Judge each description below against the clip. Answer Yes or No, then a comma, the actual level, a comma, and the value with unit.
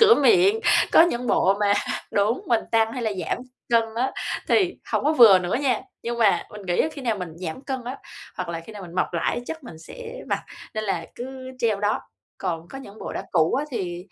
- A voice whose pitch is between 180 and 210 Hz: No, high, 225 Hz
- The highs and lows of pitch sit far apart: Yes, wide, 6.0 semitones